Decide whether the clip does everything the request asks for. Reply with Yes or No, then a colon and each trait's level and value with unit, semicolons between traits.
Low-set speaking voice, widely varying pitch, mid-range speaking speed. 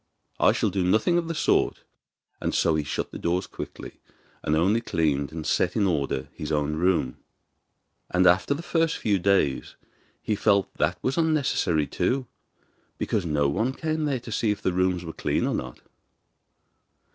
Yes: very low, 95 Hz; wide, 6.9 semitones; average, 180 wpm